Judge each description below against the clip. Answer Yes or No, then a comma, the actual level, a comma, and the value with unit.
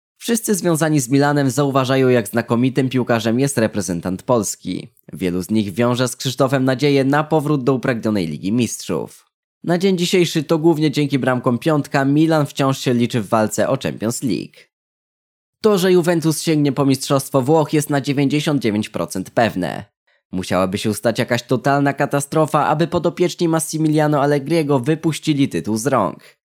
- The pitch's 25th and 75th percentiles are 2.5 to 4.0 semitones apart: No, average, 4.5 semitones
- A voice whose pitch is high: No, medium, 140 Hz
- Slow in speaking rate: No, average, 150 wpm